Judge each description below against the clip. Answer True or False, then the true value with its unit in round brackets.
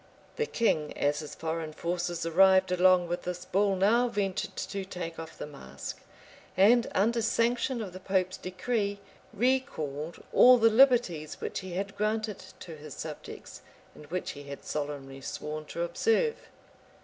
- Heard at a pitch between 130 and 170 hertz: False (185 Hz)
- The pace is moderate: True (155 wpm)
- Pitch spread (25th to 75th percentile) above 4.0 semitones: True (5.3 semitones)